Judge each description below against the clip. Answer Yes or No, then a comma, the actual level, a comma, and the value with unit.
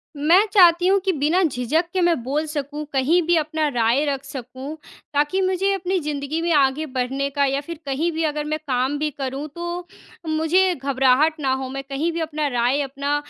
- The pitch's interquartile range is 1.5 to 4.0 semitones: Yes, average, 3.5 semitones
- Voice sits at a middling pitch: No, very high, 295 Hz